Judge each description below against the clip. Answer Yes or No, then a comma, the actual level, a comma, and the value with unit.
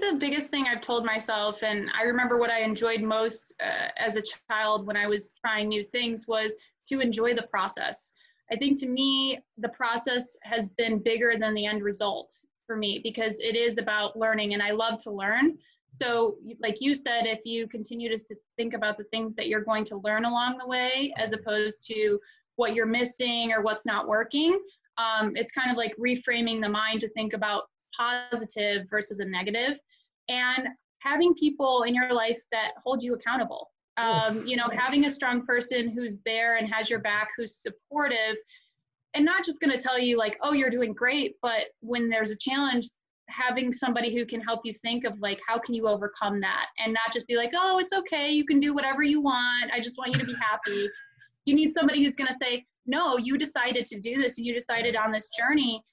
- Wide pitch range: No, average, 2.9 semitones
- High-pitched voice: Yes, high, 235 Hz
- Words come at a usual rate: No, fast, 210 wpm